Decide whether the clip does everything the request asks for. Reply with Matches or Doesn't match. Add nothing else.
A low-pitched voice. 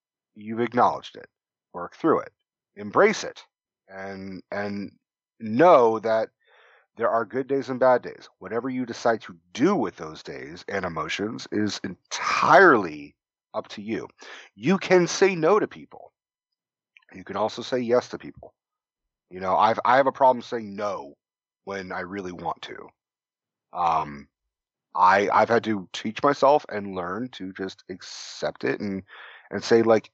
Matches